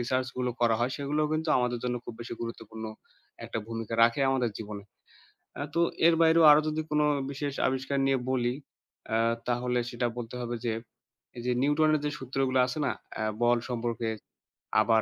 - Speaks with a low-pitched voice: Yes, low, 125 Hz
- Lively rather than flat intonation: No, average, 3.0 semitones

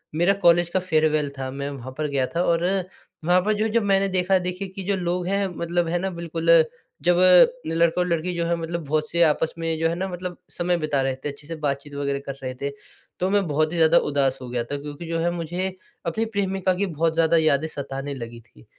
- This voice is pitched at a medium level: Yes, medium, 165 Hz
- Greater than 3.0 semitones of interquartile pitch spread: Yes, average, 3.6 semitones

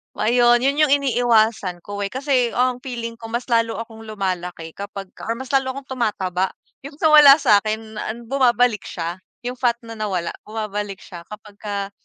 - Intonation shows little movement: No, average, 3.5 semitones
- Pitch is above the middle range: Yes, high, 225 Hz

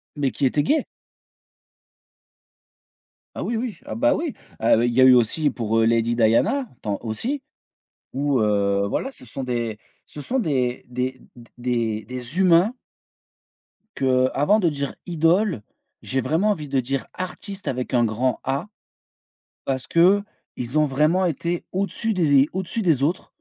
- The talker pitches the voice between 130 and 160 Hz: Yes, medium, 140 Hz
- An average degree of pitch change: No, wide, 6.9 semitones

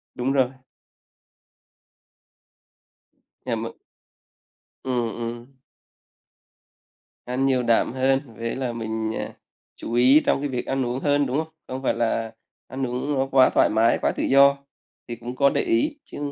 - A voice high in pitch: No, low, 130 Hz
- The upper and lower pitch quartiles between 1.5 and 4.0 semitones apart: Yes, narrow, 2.4 semitones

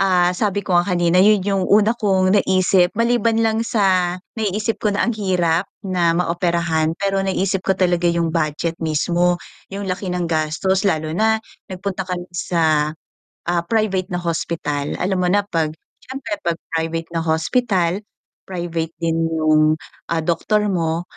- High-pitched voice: No, medium, 180 Hz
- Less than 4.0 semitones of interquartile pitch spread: Yes, average, 3.0 semitones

